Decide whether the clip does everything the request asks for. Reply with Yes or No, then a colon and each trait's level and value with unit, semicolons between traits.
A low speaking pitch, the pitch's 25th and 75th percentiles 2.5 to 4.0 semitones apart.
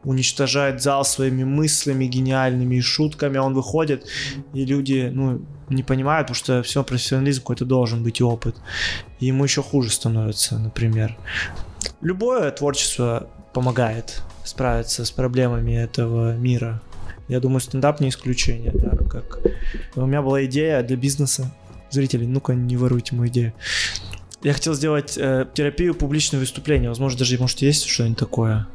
Yes: low, 130 Hz; average, 2.8 semitones